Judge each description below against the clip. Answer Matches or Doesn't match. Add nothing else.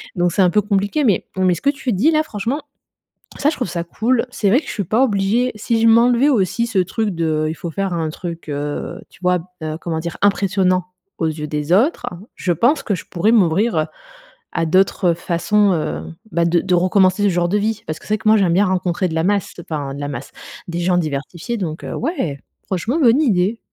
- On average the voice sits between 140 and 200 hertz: Matches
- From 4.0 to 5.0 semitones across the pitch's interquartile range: Matches